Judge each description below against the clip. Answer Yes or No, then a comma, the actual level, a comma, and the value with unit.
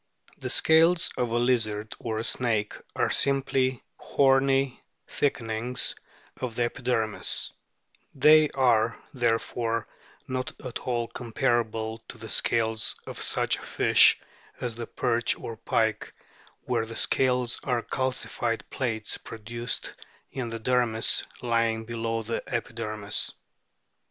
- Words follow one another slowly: Yes, slow, 120 wpm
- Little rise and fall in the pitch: Yes, narrow, 2.1 semitones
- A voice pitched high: No, low, 120 Hz